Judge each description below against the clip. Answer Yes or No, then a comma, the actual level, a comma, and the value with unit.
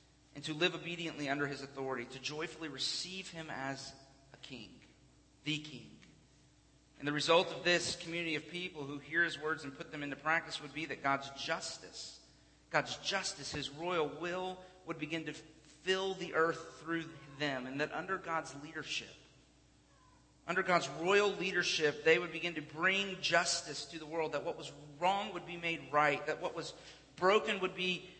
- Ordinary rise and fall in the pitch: Yes, average, 3.1 semitones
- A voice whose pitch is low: No, medium, 160 Hz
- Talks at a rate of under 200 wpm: Yes, average, 175 wpm